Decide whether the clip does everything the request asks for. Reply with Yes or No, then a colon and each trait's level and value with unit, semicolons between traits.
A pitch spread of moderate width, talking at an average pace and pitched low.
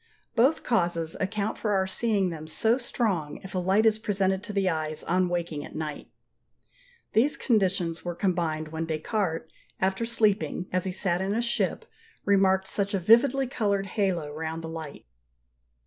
No: average, 4.2 semitones; average, 165 wpm; high, 190 Hz